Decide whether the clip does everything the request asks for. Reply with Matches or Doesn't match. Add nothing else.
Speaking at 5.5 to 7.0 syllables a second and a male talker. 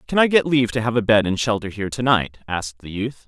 Matches